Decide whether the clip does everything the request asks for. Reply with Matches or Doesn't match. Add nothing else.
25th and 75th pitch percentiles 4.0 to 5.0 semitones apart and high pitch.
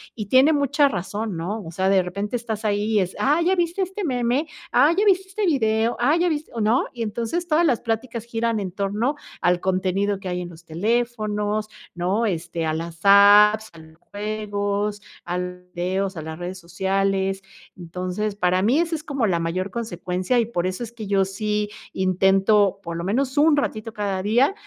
Matches